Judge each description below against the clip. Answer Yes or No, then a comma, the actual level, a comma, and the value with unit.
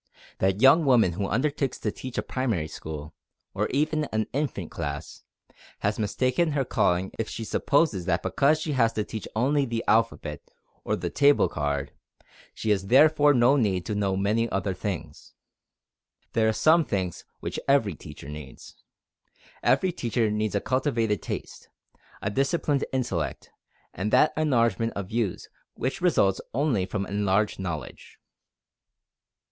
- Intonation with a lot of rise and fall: Yes, wide, 6.0 semitones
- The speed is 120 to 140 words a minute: No, average, 150 wpm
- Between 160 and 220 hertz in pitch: No, low, 110 Hz